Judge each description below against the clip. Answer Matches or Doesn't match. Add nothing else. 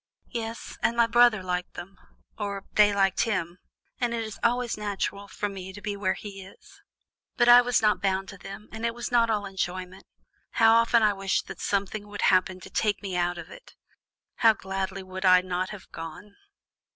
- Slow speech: Doesn't match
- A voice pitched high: Matches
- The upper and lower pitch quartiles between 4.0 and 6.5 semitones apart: Doesn't match